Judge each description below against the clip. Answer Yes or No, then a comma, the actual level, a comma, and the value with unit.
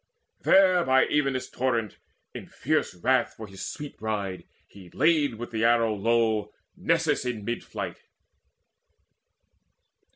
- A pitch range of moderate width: Yes, average, 3.7 semitones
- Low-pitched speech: Yes, low, 115 Hz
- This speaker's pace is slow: Yes, slow, 125 wpm